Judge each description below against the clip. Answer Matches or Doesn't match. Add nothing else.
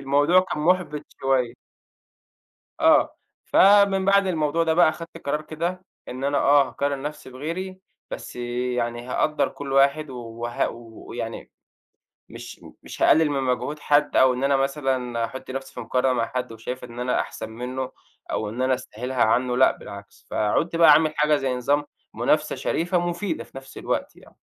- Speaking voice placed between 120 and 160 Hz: Matches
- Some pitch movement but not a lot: Matches